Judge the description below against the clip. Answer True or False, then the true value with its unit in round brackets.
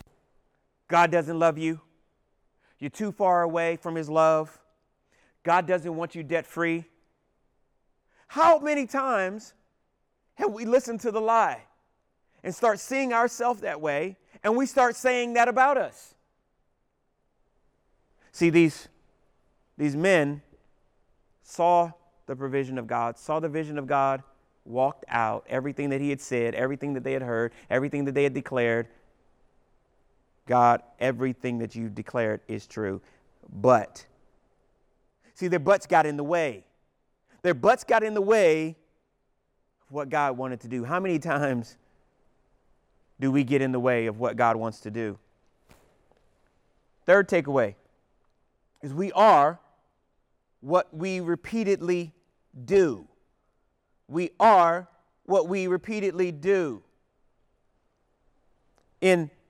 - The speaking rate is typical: False (130 wpm)